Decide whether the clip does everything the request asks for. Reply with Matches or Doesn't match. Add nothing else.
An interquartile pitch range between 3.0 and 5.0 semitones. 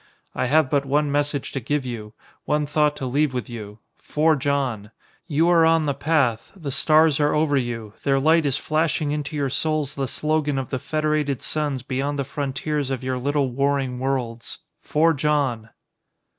Doesn't match